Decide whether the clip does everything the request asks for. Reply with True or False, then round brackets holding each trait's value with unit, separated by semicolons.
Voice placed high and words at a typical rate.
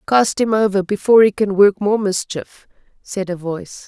True (200 Hz; 185 wpm)